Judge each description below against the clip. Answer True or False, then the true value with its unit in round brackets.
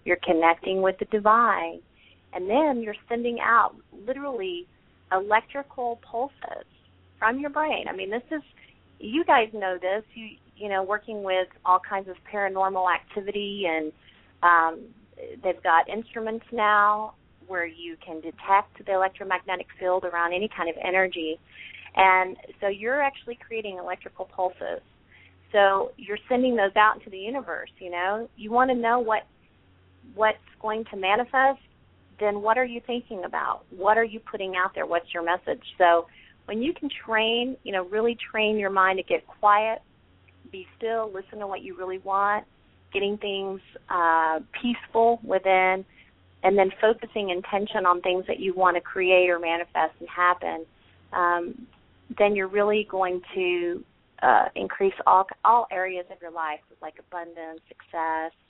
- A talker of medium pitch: False (195 Hz)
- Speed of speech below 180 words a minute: True (155 wpm)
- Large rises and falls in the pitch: False (4.1 semitones)